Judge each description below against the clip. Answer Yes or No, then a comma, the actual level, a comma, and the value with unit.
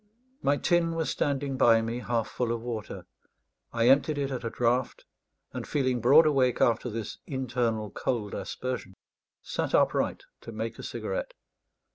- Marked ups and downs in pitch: No, average, 3.4 semitones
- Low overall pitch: Yes, low, 125 Hz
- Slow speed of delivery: No, average, 155 wpm